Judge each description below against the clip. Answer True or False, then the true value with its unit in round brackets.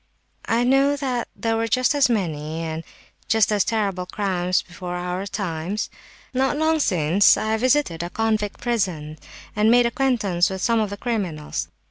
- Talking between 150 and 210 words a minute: True (160 wpm)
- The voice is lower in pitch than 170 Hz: False (210 Hz)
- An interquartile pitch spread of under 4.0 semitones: False (5.1 semitones)